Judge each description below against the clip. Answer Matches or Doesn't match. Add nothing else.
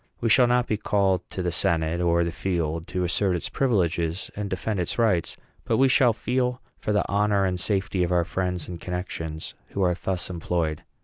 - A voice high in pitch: Doesn't match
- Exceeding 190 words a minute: Matches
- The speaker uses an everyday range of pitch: Matches